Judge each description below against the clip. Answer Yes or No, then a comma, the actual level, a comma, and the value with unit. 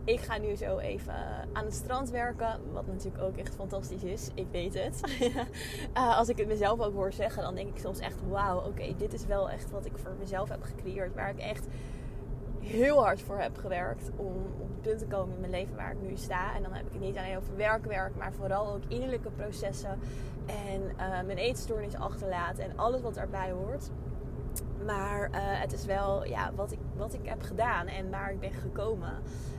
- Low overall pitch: No, high, 230 Hz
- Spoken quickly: Yes, fast, 215 wpm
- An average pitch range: Yes, average, 4.3 semitones